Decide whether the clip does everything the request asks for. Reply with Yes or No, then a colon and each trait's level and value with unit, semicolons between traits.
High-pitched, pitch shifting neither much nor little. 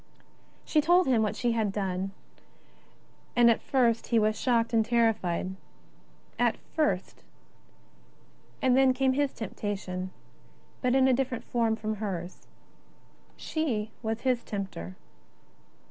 Yes: high, 230 Hz; average, 3.8 semitones